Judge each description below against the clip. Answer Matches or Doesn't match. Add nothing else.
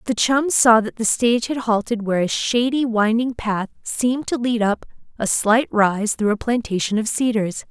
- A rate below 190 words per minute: Doesn't match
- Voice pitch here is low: Doesn't match